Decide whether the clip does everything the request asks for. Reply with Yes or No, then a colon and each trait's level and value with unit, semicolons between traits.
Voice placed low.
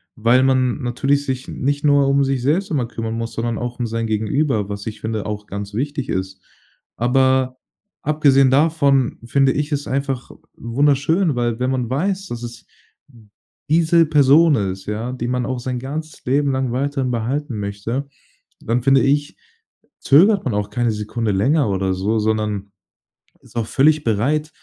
Yes: low, 130 Hz